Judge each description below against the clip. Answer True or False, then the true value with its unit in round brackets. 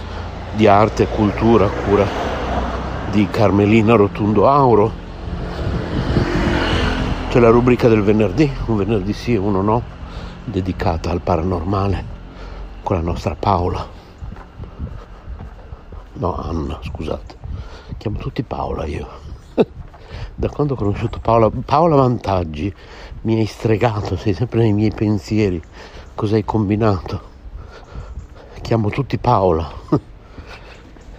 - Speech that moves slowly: True (105 wpm)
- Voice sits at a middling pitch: False (100 Hz)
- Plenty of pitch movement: False (4.1 semitones)